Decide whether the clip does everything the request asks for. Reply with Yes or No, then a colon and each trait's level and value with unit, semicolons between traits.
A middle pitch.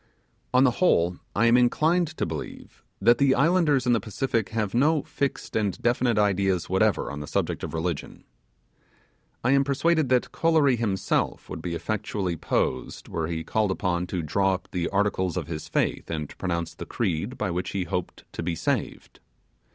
No: low, 100 Hz